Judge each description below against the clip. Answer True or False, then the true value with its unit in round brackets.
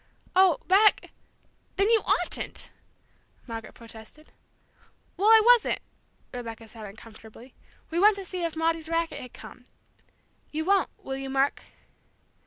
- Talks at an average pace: False (130 wpm)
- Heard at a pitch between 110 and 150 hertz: False (315 Hz)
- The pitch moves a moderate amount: False (8.5 semitones)